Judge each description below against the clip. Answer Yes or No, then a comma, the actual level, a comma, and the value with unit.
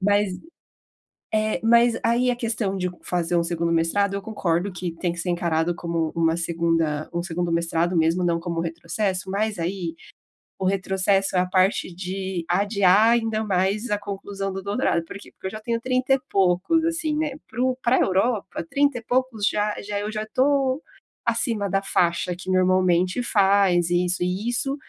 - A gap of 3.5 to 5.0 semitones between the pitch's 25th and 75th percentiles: Yes, average, 4.0 semitones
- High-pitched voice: Yes, high, 195 Hz